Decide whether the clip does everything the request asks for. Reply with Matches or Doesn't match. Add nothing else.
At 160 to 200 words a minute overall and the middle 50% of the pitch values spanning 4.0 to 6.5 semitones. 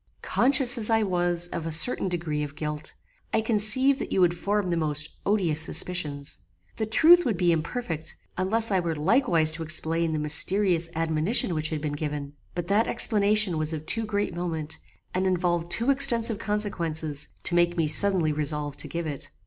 Matches